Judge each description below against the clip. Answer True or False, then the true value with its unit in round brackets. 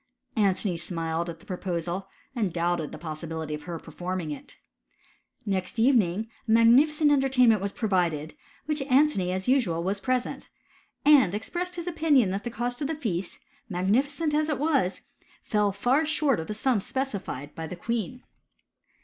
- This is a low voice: False (210 Hz)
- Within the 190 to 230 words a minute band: False (165 wpm)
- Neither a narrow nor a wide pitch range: False (7.4 semitones)